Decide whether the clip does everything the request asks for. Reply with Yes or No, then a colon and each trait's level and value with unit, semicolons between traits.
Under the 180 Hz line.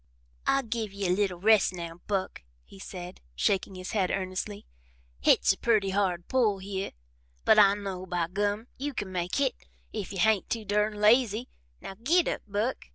No: high, 200 Hz